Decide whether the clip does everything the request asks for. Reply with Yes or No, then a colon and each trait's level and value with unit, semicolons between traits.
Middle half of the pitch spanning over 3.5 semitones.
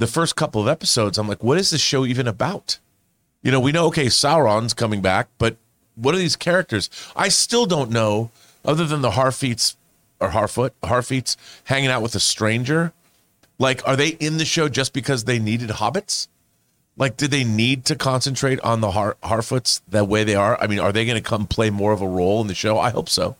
Yes: average, 4.2 semitones